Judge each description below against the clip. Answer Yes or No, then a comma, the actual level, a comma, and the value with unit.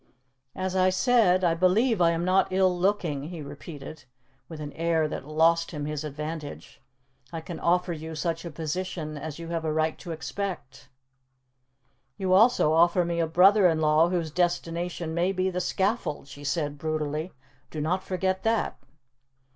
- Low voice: No, medium, 170 Hz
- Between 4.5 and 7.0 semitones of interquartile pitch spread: No, average, 3.0 semitones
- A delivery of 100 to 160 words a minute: No, average, 170 wpm